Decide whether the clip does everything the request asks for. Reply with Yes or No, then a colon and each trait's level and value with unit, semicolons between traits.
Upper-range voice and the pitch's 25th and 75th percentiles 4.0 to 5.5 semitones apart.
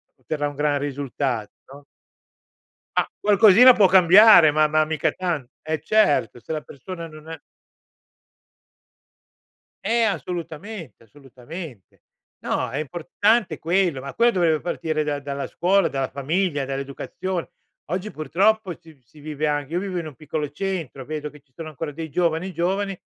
No: medium, 155 Hz; average, 4.3 semitones